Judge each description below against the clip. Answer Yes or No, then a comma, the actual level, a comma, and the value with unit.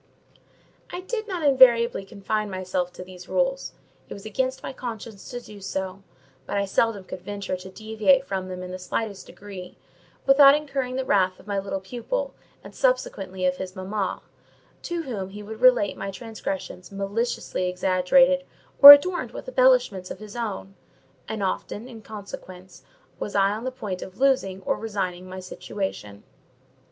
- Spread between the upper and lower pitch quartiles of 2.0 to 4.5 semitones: No, average, 5.3 semitones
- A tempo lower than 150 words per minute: No, average, 165 wpm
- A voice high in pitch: Yes, high, 205 Hz